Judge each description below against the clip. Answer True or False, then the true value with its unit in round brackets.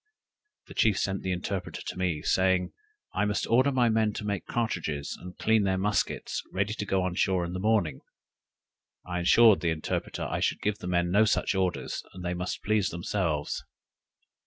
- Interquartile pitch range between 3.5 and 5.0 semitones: False (2.9 semitones)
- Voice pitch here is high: False (95 Hz)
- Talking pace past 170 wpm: True (185 wpm)